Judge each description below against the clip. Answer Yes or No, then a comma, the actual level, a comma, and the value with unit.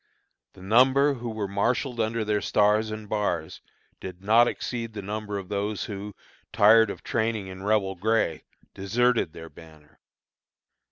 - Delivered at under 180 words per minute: Yes, average, 150 wpm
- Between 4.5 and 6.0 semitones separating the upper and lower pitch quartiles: No, average, 2.7 semitones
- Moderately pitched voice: No, low, 105 Hz